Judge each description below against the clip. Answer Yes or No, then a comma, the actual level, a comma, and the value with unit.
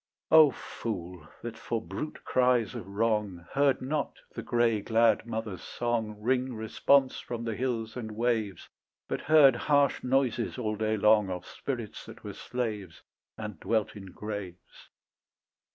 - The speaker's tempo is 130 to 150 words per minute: Yes, average, 145 wpm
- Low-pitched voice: Yes, low, 115 Hz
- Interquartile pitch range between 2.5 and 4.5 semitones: Yes, average, 2.9 semitones